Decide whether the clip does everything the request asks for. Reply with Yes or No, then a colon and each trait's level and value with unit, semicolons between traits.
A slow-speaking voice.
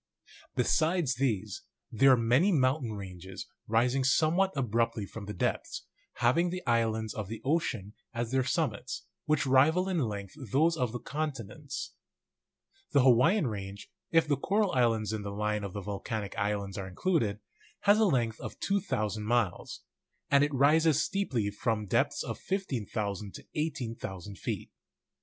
No: average, 155 wpm